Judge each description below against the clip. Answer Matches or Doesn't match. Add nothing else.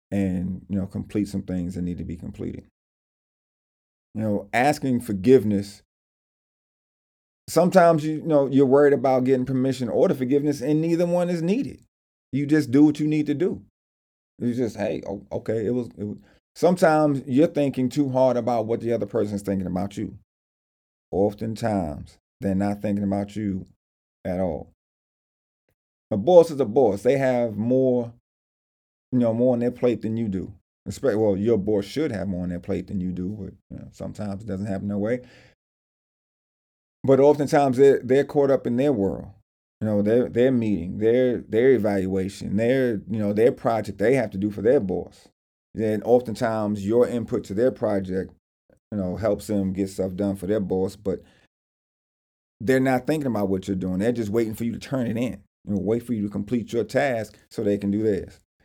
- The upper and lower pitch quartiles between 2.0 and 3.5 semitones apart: Doesn't match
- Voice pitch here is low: Matches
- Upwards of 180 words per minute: Matches